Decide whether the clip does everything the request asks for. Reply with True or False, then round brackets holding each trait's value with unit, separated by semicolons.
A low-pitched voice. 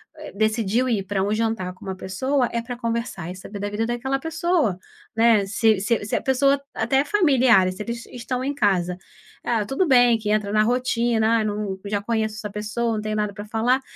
False (225 Hz)